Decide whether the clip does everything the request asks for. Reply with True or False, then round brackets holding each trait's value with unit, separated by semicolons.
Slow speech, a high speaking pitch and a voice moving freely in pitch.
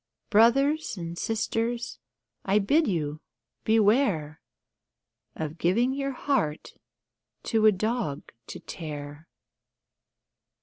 True (90 wpm; 210 Hz; 7.0 semitones)